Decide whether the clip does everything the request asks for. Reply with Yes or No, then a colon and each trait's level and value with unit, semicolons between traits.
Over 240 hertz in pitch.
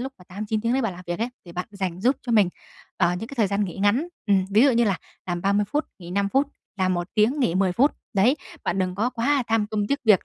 No: high, 205 Hz